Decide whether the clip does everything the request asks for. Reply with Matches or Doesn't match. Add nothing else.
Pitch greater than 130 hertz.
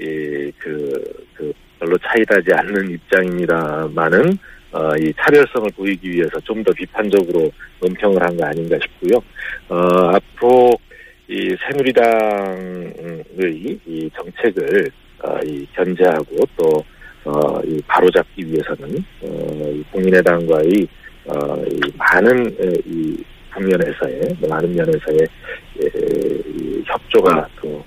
Doesn't match